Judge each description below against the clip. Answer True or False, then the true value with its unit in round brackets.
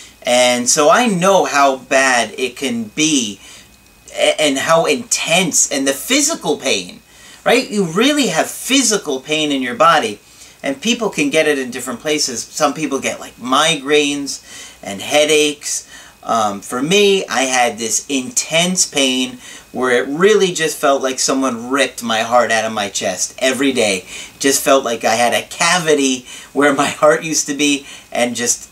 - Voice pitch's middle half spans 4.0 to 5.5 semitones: True (4.7 semitones)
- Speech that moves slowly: False (165 wpm)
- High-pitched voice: False (145 Hz)